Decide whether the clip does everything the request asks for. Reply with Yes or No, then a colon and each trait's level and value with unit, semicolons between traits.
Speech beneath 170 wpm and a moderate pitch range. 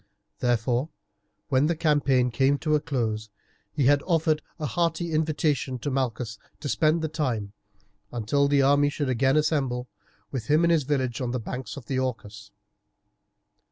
Yes: average, 160 wpm; average, 3.7 semitones